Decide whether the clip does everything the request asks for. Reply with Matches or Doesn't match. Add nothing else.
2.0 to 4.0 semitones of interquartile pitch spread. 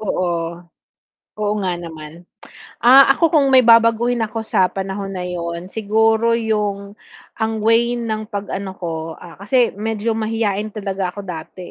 Matches